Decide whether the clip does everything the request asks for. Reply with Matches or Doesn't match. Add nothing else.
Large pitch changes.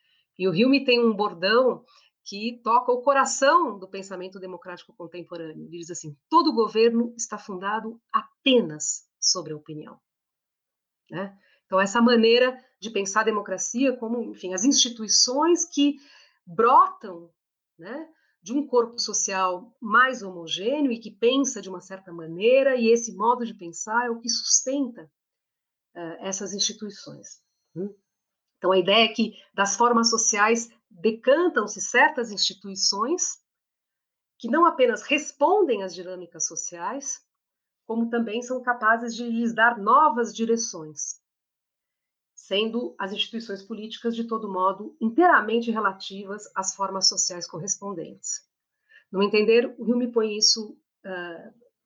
Doesn't match